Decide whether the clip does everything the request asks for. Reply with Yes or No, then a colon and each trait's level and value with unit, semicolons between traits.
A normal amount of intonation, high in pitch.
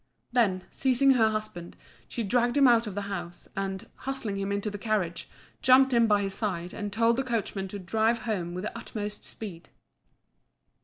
Yes: average, 3.3 semitones; high, 210 Hz